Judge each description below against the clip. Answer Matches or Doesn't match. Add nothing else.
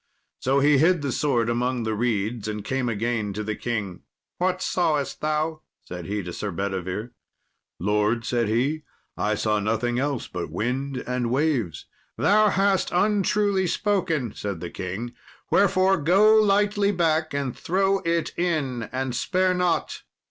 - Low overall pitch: Matches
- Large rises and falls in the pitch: Matches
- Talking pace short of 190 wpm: Matches